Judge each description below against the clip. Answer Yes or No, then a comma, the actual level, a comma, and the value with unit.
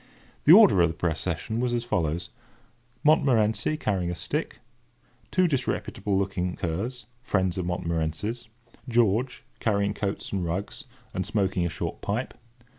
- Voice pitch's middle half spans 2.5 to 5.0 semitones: No, wide, 5.4 semitones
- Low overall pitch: Yes, low, 100 Hz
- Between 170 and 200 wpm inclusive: No, slow, 135 wpm